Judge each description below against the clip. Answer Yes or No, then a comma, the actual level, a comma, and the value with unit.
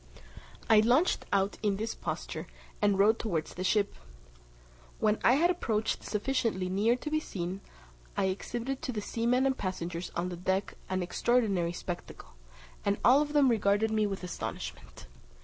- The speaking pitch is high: Yes, high, 210 Hz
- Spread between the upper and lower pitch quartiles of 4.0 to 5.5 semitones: Yes, average, 4.3 semitones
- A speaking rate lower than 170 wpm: Yes, average, 160 wpm